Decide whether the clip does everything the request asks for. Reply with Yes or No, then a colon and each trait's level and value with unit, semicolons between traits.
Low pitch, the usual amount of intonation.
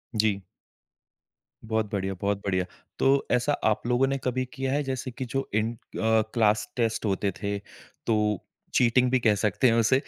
Yes: low, 115 Hz; average, 3.4 semitones